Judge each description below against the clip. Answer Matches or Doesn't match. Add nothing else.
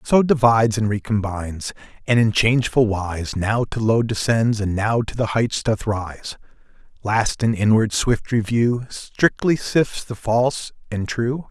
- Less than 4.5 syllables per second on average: Matches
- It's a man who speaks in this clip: Matches